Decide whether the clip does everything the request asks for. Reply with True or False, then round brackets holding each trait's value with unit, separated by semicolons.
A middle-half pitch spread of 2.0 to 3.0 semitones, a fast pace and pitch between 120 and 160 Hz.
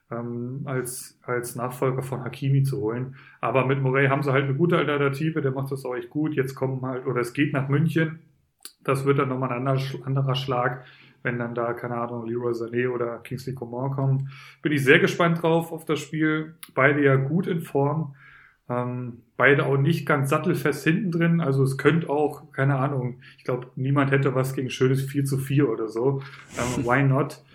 True (2.6 semitones; 200 wpm; 135 Hz)